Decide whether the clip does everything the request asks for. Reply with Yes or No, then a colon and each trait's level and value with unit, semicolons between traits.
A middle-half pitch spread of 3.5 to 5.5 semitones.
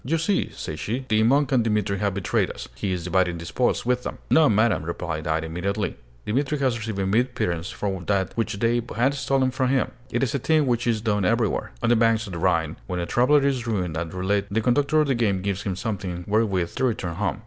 Yes: average, 5.1 semitones